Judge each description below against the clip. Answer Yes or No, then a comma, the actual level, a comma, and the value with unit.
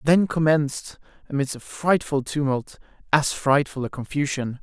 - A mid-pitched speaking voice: Yes, medium, 145 Hz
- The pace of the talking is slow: Yes, slow, 130 wpm